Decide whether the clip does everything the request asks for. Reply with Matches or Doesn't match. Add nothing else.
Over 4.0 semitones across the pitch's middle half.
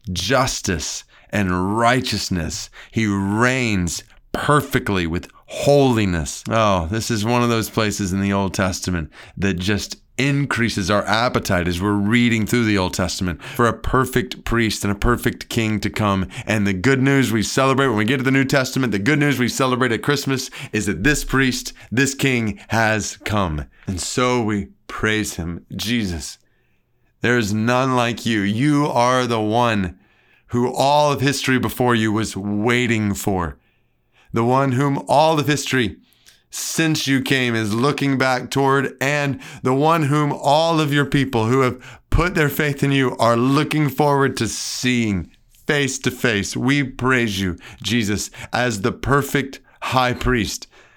Matches